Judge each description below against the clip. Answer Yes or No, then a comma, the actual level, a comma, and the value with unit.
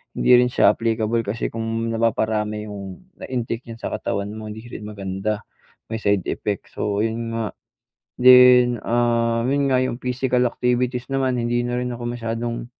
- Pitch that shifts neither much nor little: No, narrow, 2.2 semitones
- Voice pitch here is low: Yes, low, 115 Hz